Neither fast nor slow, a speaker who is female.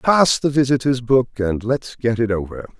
No: average, 195 wpm; male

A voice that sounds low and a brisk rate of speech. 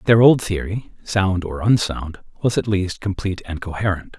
No: very low, 95 Hz; average, 170 wpm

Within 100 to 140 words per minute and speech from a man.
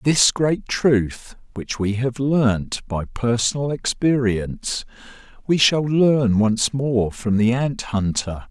Yes: slow, 135 wpm; male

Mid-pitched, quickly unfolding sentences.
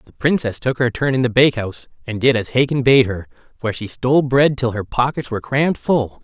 No: low, 125 Hz; fast, 230 wpm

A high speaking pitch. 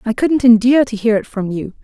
Yes: high, 230 Hz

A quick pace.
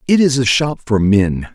Yes: fast, 235 wpm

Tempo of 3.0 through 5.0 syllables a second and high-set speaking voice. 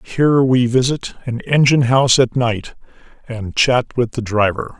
No: 4.8 syllables/s; low, 125 Hz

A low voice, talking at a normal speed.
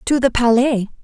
No: high, 245 Hz; average, 175 wpm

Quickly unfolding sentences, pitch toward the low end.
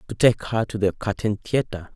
Yes: fast, 215 wpm; low, 105 Hz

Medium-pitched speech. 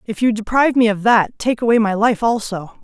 No: high, 220 Hz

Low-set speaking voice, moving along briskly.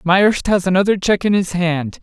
No: medium, 185 Hz; fast, 210 wpm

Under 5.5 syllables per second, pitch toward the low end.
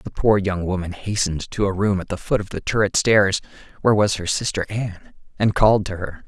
No: 5.7 syllables/s; very low, 95 Hz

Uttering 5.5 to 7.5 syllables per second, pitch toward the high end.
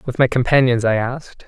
No: 5.9 syllables/s; low, 125 Hz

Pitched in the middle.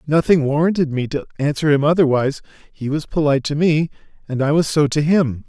Yes: medium, 150 Hz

